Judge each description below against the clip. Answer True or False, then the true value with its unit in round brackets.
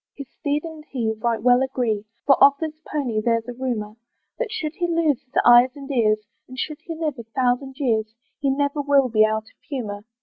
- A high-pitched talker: True (260 Hz)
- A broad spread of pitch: False (4.1 semitones)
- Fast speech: True (210 wpm)